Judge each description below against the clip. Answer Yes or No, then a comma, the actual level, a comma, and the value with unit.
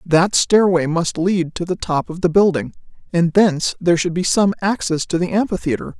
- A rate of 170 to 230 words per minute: Yes, average, 200 wpm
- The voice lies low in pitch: No, medium, 180 Hz